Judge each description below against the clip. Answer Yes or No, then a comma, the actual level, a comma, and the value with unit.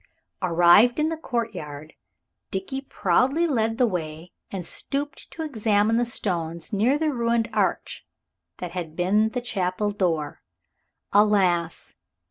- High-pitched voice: Yes, high, 210 Hz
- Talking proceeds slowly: Yes, slow, 125 wpm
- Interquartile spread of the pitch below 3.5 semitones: No, wide, 5.5 semitones